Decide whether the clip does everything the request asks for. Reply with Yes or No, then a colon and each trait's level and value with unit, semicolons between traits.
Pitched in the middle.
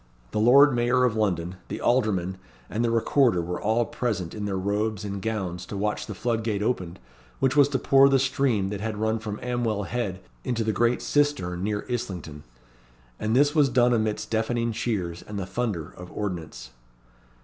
No: low, 110 Hz